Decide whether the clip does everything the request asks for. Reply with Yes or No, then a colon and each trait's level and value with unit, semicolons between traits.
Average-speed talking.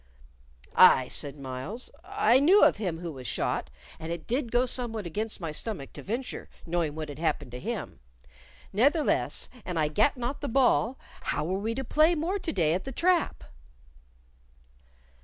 Yes: average, 175 wpm